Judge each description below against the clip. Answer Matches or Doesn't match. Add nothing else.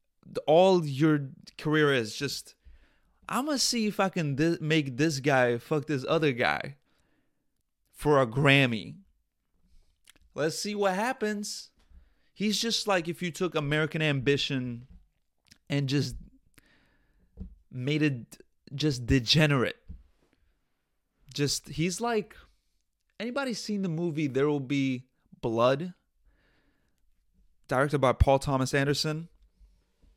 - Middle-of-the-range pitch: Matches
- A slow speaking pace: Matches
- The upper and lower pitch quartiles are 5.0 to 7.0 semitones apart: Matches